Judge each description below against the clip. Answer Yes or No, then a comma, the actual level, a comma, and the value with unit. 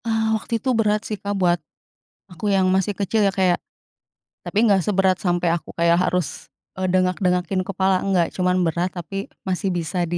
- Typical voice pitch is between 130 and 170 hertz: No, medium, 185 Hz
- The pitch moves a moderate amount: No, narrow, 2.1 semitones